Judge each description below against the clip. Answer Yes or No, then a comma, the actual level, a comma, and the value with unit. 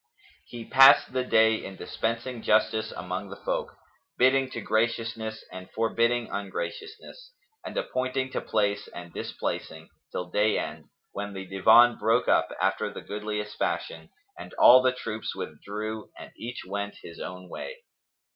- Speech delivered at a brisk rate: No, average, 145 wpm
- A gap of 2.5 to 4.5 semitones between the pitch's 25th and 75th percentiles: Yes, average, 3.3 semitones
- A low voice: Yes, low, 110 Hz